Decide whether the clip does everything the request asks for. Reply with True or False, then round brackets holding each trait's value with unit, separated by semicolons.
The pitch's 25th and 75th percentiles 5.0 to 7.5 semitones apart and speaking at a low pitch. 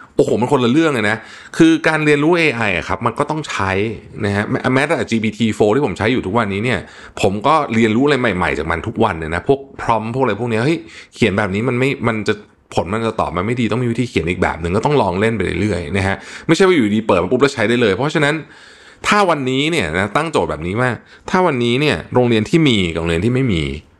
True (5.3 semitones; 115 Hz)